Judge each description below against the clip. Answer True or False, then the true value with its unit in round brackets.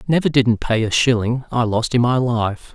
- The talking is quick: True (220 wpm)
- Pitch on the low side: True (120 Hz)